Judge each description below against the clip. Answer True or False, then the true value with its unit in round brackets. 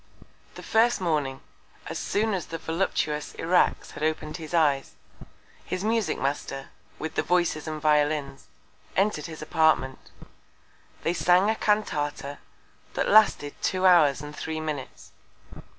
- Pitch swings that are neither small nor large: True (3.7 semitones)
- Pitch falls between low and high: True (160 Hz)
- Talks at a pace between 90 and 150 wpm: True (135 wpm)